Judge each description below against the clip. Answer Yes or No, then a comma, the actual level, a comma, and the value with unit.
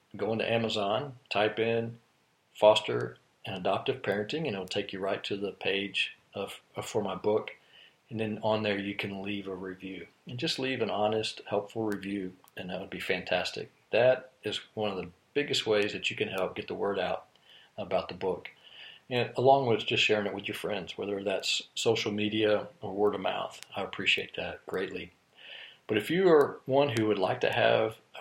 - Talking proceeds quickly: No, average, 195 wpm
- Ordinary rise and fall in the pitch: No, narrow, 2.3 semitones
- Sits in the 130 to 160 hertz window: No, low, 105 Hz